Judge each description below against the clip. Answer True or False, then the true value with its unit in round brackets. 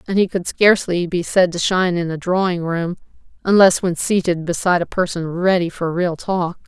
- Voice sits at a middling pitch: True (175 Hz)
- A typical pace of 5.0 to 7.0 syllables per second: True (5.3 syllables/s)